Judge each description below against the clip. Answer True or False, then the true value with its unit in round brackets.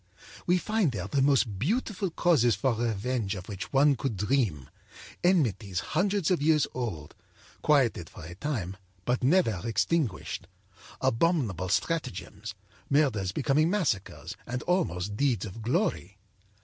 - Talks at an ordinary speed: False (130 wpm)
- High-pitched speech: False (125 Hz)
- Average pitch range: False (7.4 semitones)